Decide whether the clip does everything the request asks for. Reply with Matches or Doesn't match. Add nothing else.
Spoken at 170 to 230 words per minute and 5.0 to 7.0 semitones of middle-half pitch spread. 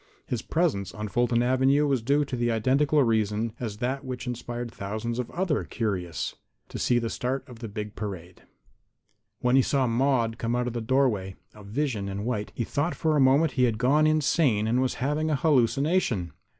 Doesn't match